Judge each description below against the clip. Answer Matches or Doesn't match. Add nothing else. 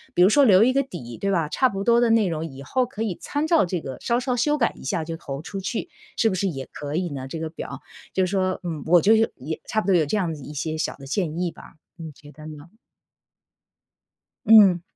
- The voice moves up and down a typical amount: Doesn't match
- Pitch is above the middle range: Doesn't match